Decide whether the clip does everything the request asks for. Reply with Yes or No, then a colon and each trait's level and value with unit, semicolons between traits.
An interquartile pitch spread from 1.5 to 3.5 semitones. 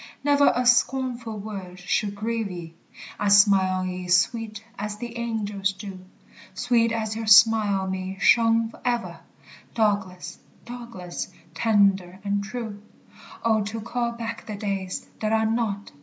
Yes: average, 2.9 semitones